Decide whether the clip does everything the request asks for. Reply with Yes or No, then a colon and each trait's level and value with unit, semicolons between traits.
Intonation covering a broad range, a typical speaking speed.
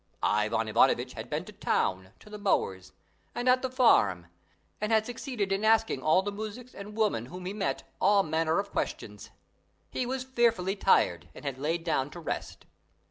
Yes: wide, 8.4 semitones; average, 185 wpm